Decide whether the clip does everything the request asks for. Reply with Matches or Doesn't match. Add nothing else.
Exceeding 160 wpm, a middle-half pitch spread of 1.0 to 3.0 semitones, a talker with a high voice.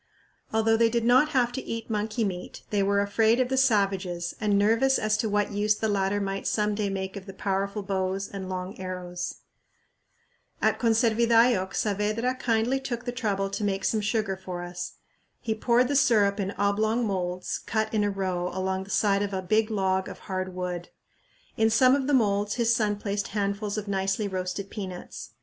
Matches